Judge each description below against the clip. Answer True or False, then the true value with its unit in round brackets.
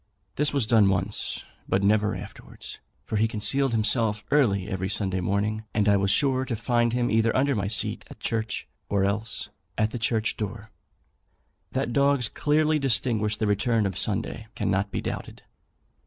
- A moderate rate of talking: True (170 wpm)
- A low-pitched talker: True (110 Hz)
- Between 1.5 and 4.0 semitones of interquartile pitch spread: True (2.9 semitones)